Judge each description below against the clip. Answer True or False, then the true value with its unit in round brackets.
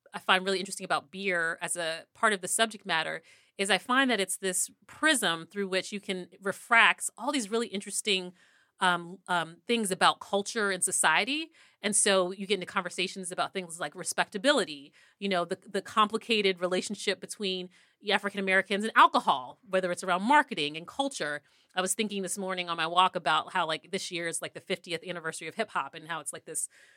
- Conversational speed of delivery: True (195 wpm)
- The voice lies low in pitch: False (190 Hz)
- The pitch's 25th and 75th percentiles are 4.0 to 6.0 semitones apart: False (2.5 semitones)